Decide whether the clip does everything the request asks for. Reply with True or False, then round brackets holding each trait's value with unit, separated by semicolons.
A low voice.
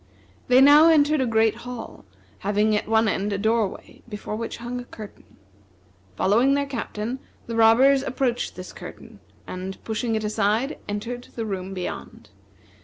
False (225 Hz)